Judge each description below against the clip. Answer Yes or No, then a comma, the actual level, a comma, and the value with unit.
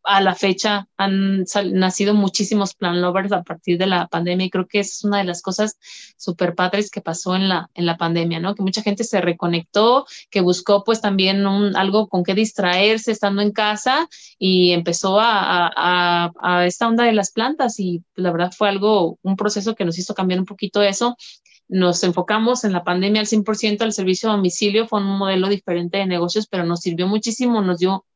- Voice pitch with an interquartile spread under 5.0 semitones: Yes, average, 2.8 semitones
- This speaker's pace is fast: Yes, fast, 205 wpm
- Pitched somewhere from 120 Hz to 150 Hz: No, high, 195 Hz